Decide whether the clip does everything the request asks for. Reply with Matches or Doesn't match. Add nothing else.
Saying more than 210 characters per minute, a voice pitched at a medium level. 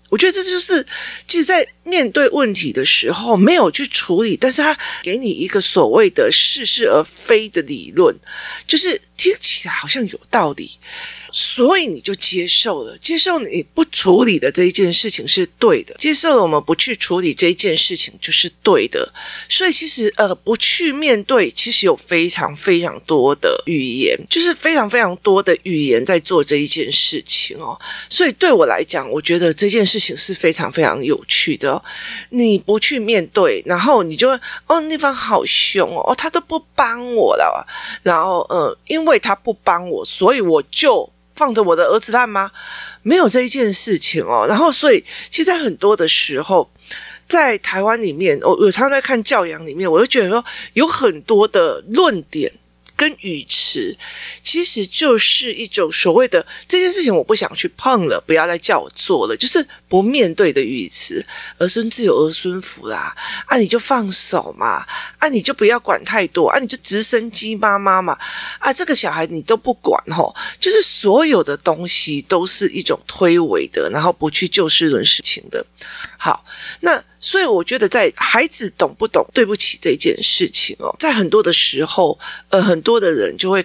Doesn't match